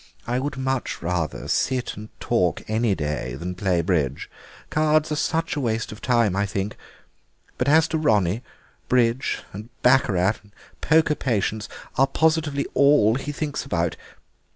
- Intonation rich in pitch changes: Yes, wide, 6.4 semitones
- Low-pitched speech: Yes, low, 115 Hz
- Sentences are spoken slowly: No, average, 155 wpm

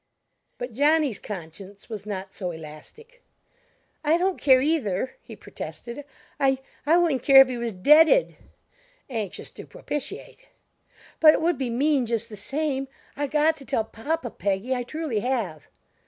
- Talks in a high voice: Yes, very high, 260 Hz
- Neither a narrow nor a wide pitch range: No, wide, 6.3 semitones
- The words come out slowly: No, average, 155 wpm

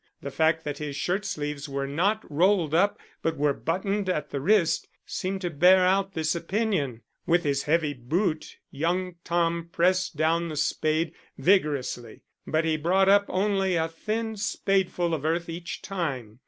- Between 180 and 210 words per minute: No, average, 165 wpm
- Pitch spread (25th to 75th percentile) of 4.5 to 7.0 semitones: No, average, 3.9 semitones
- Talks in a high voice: No, medium, 170 Hz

